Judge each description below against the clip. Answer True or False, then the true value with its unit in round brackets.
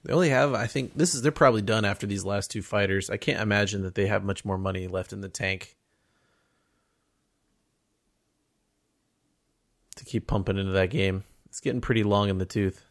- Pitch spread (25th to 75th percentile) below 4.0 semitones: True (2.8 semitones)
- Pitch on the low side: True (100 Hz)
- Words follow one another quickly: False (190 wpm)